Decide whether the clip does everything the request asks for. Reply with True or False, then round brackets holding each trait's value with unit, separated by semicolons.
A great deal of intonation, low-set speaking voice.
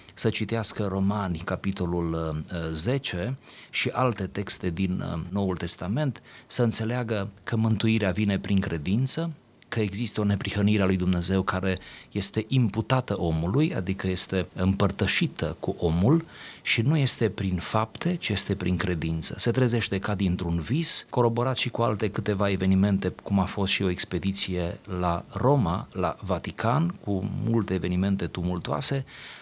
False (3.8 semitones; 100 Hz)